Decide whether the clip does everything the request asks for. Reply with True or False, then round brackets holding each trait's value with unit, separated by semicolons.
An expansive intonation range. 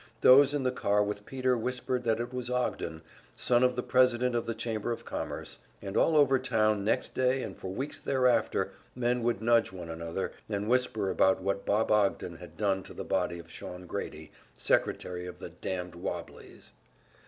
False (4.9 semitones)